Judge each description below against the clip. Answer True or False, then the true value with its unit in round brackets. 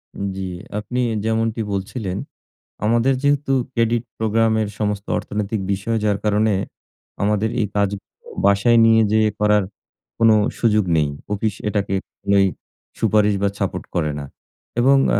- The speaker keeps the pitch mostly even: True (2.1 semitones)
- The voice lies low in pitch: True (105 Hz)